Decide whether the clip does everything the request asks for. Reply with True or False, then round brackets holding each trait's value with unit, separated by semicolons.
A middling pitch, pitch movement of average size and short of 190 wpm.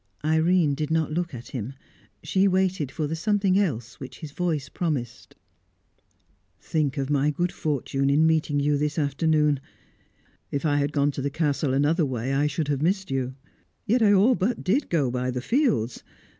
True (150 Hz; 4.1 semitones; 180 wpm)